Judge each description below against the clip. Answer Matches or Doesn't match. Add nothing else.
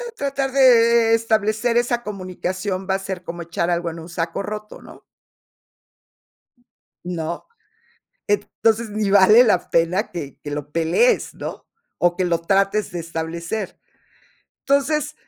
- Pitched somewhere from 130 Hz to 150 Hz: Doesn't match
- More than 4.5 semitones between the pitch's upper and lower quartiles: Matches